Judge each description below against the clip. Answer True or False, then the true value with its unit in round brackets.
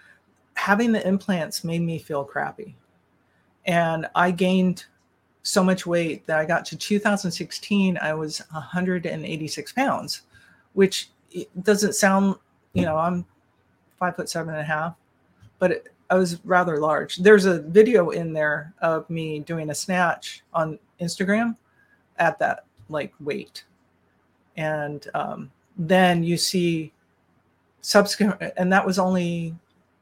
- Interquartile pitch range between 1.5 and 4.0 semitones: True (3.6 semitones)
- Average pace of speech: False (130 wpm)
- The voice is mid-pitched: True (170 Hz)